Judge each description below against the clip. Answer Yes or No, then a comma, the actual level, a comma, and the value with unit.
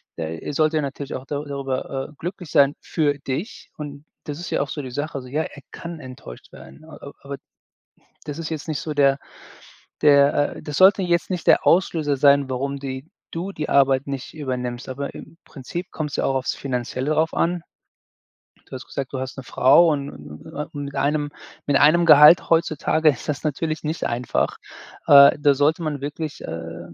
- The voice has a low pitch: No, medium, 145 Hz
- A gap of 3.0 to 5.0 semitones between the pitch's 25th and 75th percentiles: No, narrow, 2.5 semitones